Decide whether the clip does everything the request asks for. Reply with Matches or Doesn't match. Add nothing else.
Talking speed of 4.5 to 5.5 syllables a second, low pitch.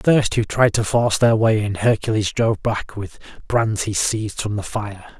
Matches